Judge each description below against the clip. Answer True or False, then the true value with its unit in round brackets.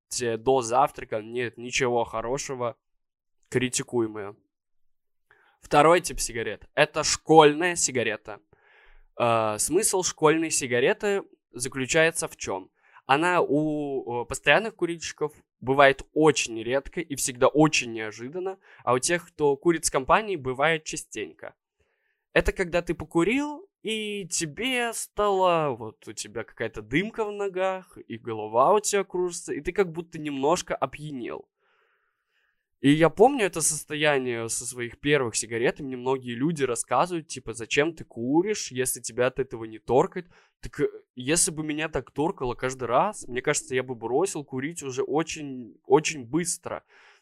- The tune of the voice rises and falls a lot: True (5.9 semitones)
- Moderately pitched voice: True (150 Hz)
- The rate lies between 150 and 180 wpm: False (130 wpm)